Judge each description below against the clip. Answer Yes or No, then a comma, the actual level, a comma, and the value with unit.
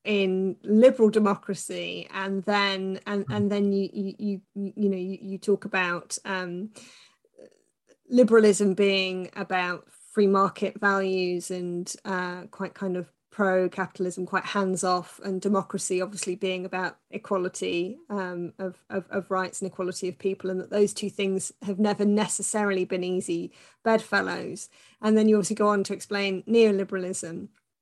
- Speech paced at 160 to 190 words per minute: No, average, 145 wpm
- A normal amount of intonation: No, narrow, 1.7 semitones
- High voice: Yes, high, 195 Hz